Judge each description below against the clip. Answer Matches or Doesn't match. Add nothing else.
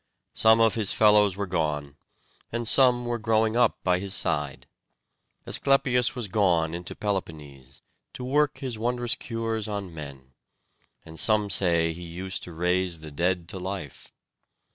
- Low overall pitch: Matches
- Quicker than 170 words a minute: Doesn't match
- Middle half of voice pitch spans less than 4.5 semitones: Doesn't match